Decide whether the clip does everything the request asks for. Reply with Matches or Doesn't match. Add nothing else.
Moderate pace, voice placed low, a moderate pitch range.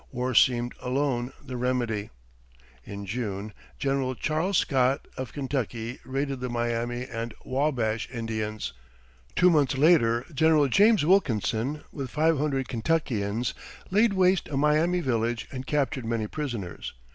Doesn't match